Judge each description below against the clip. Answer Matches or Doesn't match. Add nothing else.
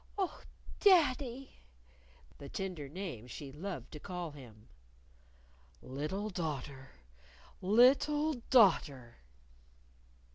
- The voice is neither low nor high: Matches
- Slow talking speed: Matches